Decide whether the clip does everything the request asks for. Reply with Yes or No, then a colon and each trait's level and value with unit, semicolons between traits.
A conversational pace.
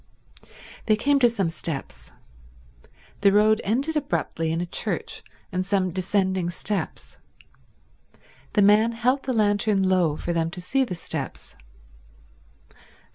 No: slow, 130 wpm